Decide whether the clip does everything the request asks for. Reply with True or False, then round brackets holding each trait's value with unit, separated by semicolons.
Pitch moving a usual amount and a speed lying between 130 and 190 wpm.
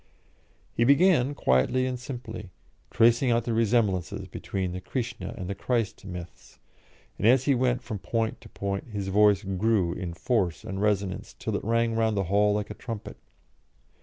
True (3.5 semitones; 170 wpm)